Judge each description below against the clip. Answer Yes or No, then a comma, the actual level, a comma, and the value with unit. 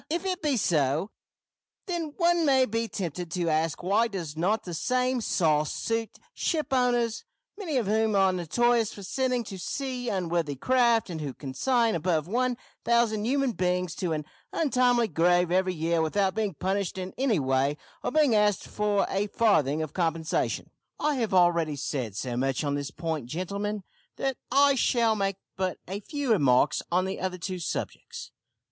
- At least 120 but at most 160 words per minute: No, average, 170 wpm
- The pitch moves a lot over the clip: Yes, wide, 6.5 semitones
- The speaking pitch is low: No, high, 195 Hz